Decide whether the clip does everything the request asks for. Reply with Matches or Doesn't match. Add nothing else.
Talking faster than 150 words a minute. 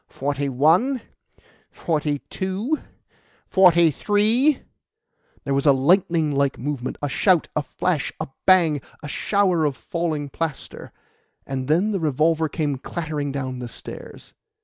Doesn't match